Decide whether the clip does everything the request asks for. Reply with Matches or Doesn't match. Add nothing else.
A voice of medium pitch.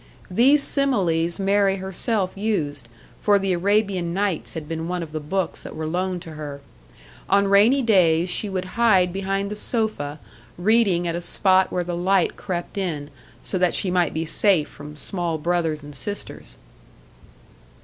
Matches